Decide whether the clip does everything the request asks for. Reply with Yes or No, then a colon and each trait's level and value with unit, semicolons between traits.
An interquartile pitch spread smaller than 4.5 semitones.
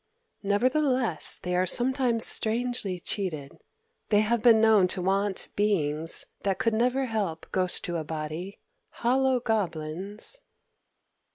No: average, 4.9 semitones